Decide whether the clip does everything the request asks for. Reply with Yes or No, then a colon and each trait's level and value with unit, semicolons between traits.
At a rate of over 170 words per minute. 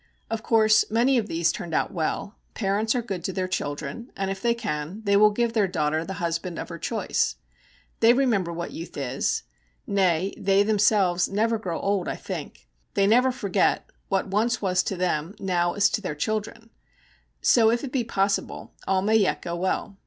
Yes: average, 190 wpm